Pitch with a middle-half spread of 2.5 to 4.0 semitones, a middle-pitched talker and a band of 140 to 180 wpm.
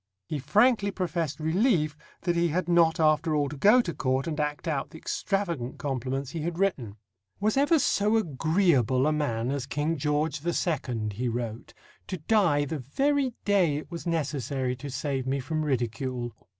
No: average, 4.5 semitones; medium, 155 Hz; average, 175 wpm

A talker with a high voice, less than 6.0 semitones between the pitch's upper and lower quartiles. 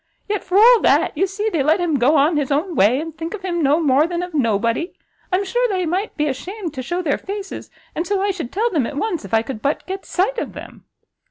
Yes: very high, 340 Hz; wide, 5.4 semitones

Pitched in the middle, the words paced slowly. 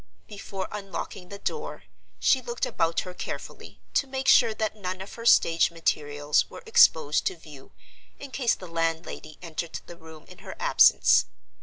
No: medium, 180 Hz; average, 165 wpm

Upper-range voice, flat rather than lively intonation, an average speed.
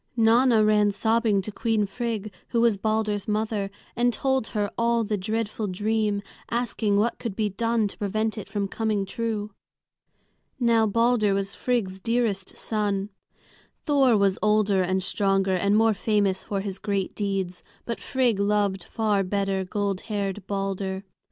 Yes: high, 210 Hz; narrow, 2.3 semitones; average, 155 wpm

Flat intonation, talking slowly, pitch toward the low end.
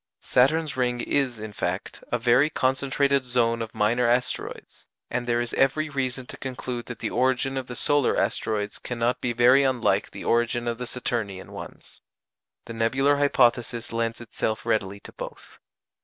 No: narrow, 2.2 semitones; average, 165 wpm; low, 125 Hz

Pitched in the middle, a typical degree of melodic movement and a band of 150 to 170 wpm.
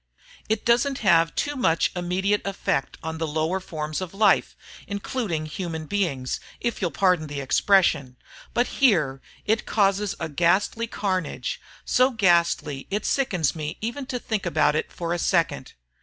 Yes: medium, 180 Hz; average, 4.8 semitones; average, 155 wpm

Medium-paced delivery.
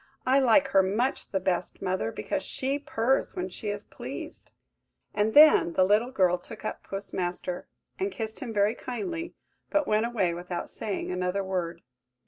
Yes: average, 170 wpm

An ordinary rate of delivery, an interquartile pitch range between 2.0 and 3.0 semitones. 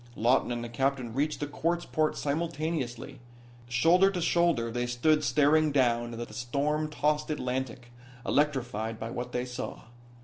No: average, 150 wpm; average, 4.1 semitones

